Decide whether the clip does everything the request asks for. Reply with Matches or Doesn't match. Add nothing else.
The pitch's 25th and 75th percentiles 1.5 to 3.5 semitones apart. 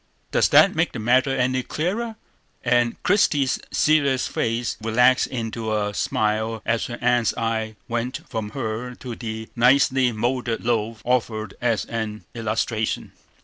Matches